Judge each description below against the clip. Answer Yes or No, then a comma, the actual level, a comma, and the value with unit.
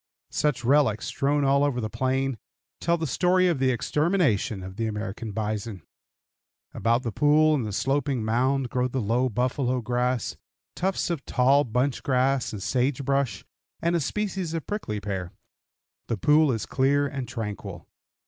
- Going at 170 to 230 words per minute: No, average, 160 wpm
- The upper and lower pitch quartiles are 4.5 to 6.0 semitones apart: No, average, 4.1 semitones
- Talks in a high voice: No, low, 130 Hz